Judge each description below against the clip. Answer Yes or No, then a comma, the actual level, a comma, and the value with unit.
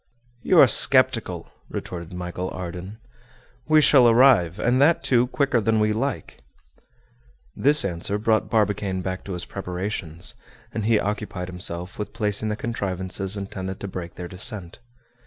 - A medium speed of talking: Yes, average, 145 wpm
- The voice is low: Yes, low, 100 Hz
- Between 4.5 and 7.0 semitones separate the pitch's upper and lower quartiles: No, average, 4.1 semitones